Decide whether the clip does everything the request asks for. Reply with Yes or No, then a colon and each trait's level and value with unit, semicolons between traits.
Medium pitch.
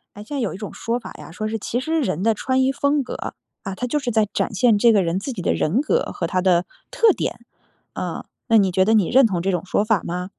No: high, 215 Hz